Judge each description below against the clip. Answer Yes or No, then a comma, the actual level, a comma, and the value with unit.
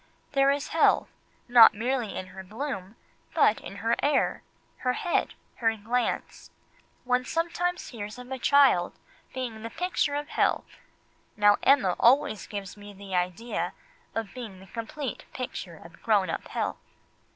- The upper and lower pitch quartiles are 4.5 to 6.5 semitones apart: Yes, average, 5.0 semitones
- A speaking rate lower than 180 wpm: Yes, average, 150 wpm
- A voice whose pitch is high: Yes, high, 230 Hz